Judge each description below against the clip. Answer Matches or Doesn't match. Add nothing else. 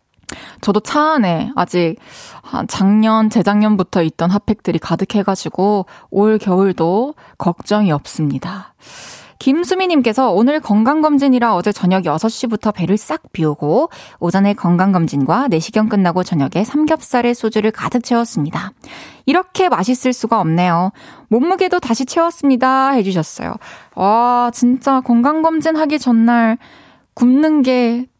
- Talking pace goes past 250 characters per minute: Matches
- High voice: Matches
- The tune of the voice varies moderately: Doesn't match